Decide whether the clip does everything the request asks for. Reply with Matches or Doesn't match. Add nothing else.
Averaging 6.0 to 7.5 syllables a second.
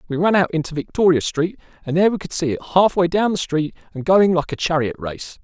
Matches